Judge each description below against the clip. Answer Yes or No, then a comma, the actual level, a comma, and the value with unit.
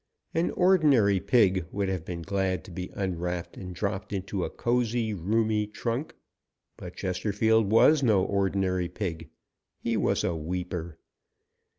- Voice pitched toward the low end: Yes, very low, 95 Hz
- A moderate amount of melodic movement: Yes, average, 3.5 semitones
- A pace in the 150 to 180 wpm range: No, slow, 135 wpm